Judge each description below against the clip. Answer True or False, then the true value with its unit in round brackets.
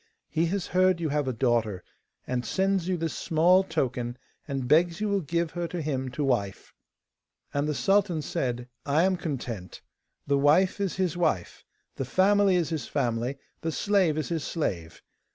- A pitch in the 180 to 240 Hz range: False (155 Hz)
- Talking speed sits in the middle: True (175 wpm)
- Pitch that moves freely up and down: True (5.8 semitones)